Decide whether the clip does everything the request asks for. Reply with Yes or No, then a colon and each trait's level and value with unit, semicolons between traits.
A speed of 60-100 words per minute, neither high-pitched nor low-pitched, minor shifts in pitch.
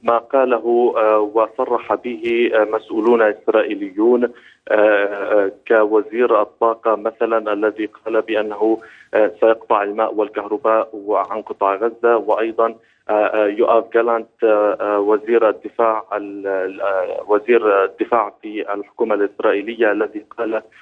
No: average, 85 wpm; low, 110 Hz; narrow, 1.7 semitones